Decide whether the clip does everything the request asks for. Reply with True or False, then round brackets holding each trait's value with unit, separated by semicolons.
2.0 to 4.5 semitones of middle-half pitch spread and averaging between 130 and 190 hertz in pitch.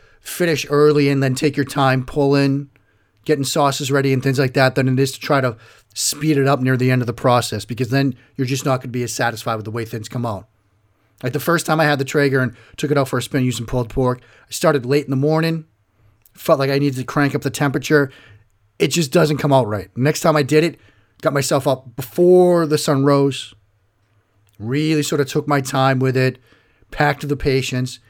True (3.3 semitones; 135 Hz)